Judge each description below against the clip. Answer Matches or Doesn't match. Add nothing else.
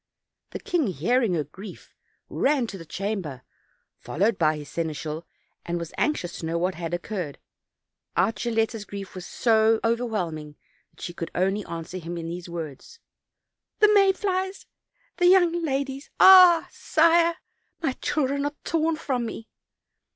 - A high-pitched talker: Matches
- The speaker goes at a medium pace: Matches